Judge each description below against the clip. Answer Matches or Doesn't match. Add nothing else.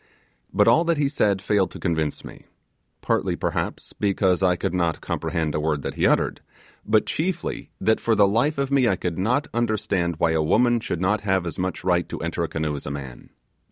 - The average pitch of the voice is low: Matches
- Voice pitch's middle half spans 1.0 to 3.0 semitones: Doesn't match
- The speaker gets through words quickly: Matches